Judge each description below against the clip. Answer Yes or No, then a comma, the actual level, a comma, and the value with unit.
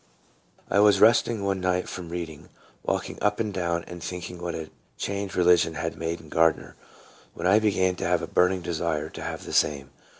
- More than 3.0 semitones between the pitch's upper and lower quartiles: No, average, 2.7 semitones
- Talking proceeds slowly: No, average, 195 wpm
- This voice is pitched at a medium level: No, very low, 90 Hz